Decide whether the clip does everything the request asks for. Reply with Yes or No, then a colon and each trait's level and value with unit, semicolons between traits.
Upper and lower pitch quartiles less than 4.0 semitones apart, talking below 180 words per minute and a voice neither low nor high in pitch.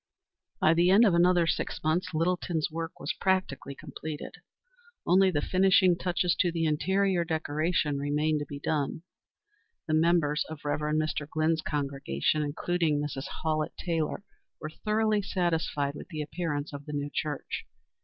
Yes: average, 3.1 semitones; average, 150 wpm; medium, 160 Hz